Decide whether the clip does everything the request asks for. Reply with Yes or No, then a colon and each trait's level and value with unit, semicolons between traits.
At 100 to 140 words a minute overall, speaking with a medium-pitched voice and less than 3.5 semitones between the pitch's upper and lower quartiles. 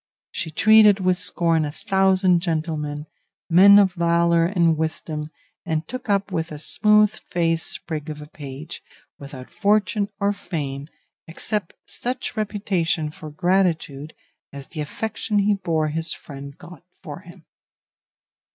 No: slow, 135 wpm; medium, 170 Hz; average, 4.4 semitones